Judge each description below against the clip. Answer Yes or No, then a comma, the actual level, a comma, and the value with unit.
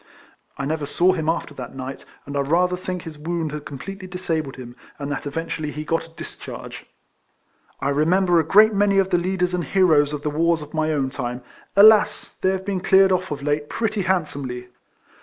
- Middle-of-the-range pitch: Yes, medium, 165 Hz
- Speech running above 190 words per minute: Yes, average, 200 wpm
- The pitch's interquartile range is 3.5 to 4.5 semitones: Yes, average, 4.2 semitones